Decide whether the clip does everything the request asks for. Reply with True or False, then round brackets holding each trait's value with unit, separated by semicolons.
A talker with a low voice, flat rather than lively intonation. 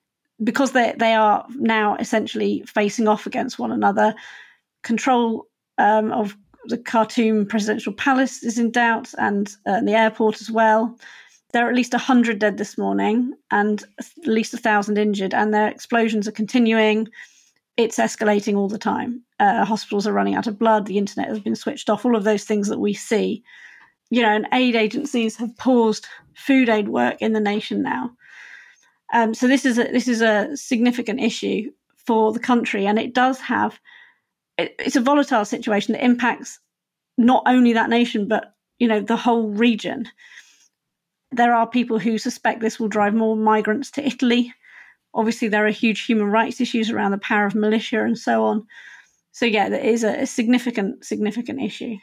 False (225 Hz; 2.2 semitones)